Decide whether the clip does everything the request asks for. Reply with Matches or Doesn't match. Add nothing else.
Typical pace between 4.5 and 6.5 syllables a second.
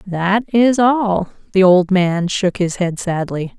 Doesn't match